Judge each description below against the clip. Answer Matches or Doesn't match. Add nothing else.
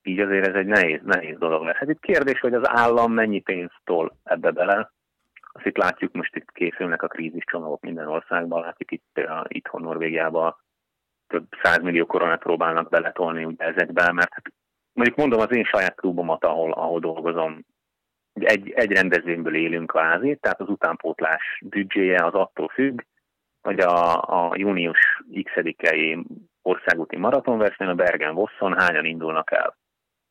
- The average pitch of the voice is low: Matches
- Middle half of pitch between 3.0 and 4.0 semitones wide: Matches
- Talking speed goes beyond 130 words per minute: Matches